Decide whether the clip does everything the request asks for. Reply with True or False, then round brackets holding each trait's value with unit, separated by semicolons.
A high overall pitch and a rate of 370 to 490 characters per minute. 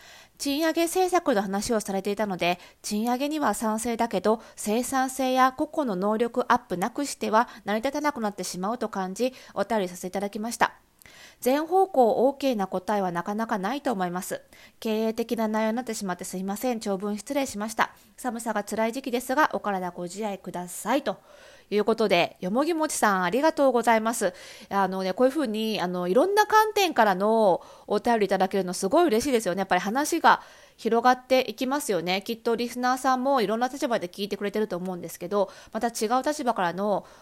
True (225 Hz; 415 characters per minute)